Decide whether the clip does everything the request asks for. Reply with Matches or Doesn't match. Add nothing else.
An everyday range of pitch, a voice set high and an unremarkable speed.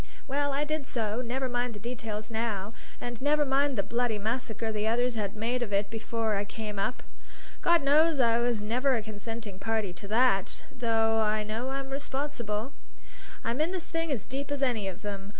Matches